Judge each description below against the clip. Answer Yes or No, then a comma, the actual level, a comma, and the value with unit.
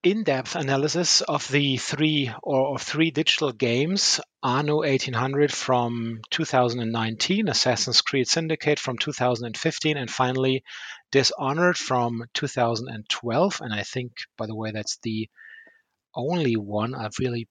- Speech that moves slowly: Yes, slow, 125 wpm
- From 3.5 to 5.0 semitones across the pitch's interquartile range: Yes, average, 4.3 semitones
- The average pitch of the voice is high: No, low, 130 Hz